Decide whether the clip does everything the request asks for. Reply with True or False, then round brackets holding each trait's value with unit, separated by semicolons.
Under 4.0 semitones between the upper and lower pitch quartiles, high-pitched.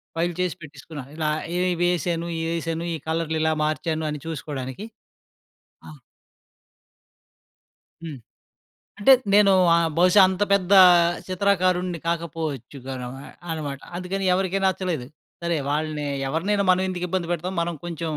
False (2.9 semitones; 170 Hz)